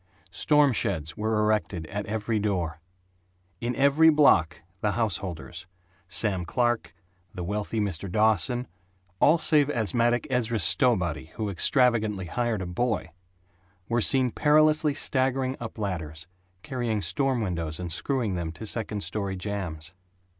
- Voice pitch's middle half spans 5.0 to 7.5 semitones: Yes, wide, 5.5 semitones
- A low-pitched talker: Yes, low, 105 Hz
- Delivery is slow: Yes, slow, 130 wpm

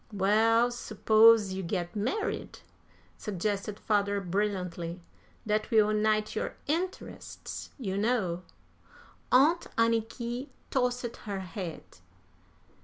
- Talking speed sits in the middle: No, slow, 95 wpm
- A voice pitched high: Yes, high, 215 Hz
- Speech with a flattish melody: No, average, 3.2 semitones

